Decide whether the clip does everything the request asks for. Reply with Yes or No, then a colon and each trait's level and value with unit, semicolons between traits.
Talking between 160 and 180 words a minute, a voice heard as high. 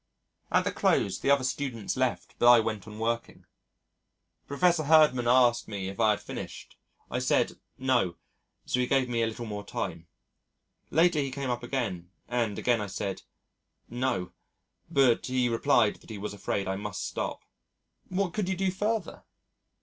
No: average, 170 wpm; low, 120 Hz